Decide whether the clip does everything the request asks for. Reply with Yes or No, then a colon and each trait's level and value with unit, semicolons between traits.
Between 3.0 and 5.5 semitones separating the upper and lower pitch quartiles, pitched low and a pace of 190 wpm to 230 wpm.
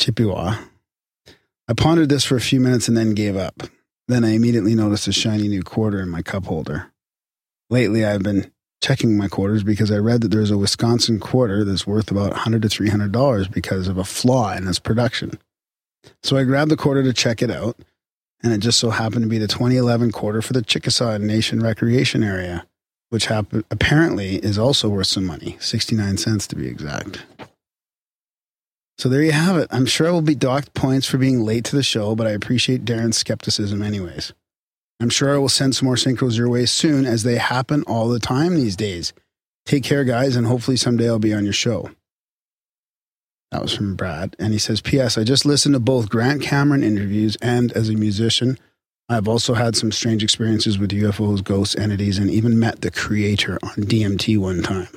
Yes: average, 3.3 semitones; low, 115 Hz; average, 200 wpm